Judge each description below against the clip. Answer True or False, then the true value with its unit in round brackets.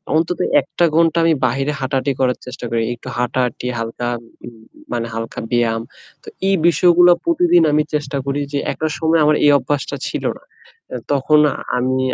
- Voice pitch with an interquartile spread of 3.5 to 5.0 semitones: True (4.5 semitones)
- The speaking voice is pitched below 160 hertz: True (135 Hz)